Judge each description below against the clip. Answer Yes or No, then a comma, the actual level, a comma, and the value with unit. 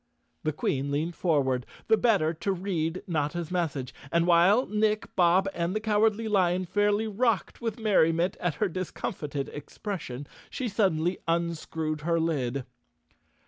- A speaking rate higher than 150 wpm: No, average, 145 wpm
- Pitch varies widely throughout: No, average, 4.8 semitones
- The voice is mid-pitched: Yes, medium, 175 Hz